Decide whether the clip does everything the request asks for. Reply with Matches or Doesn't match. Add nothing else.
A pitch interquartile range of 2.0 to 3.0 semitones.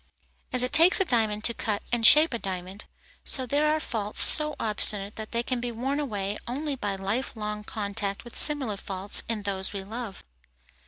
Doesn't match